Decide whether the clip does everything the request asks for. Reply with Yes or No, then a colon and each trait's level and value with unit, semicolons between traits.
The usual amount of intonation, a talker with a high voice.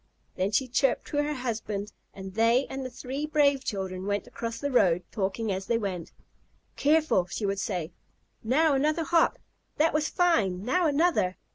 No: wide, 6.9 semitones; high, 235 Hz